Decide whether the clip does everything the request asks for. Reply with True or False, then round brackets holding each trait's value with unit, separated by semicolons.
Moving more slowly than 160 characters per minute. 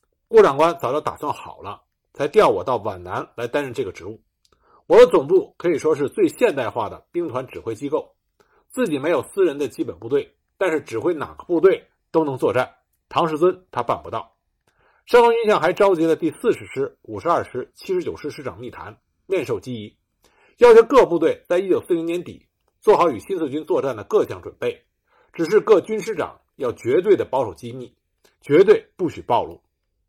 False (285 characters per minute)